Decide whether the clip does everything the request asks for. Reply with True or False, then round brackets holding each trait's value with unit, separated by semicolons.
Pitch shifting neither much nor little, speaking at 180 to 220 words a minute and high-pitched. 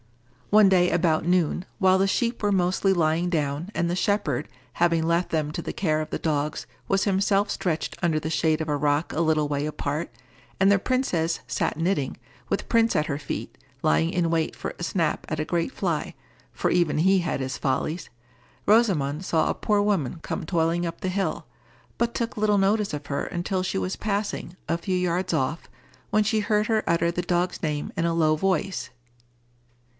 False (3.9 semitones; 195 wpm; 170 Hz)